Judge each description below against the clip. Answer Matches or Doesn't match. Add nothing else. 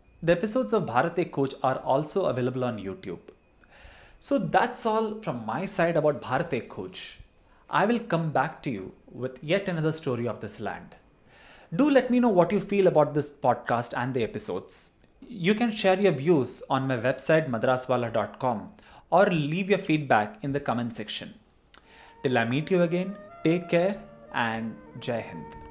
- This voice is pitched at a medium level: Matches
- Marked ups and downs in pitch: Matches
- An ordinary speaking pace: Matches